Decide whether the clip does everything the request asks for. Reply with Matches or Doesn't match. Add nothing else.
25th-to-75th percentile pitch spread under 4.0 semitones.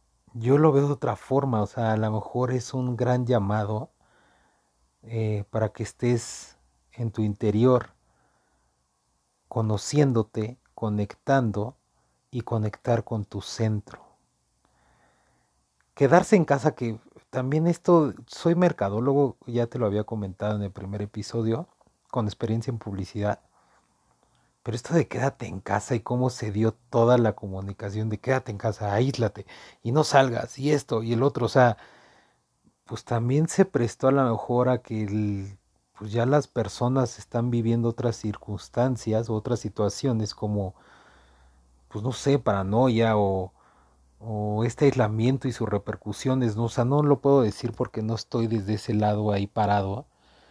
Matches